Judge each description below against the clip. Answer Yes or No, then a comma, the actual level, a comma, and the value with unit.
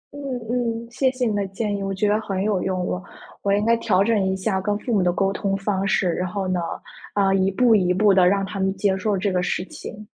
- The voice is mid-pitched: No, high, 195 Hz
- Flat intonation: Yes, narrow, 2.0 semitones